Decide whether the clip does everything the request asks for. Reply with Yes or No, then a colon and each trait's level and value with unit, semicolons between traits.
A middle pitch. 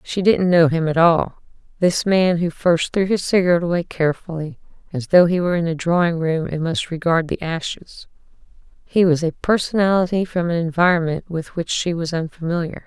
Yes: medium, 170 Hz